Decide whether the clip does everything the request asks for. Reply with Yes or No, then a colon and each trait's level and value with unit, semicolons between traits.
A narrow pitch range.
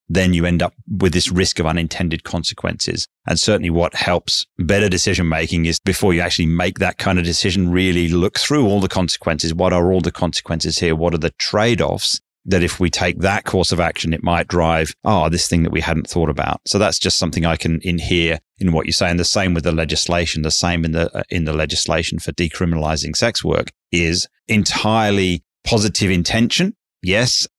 Yes: narrow, 2.3 semitones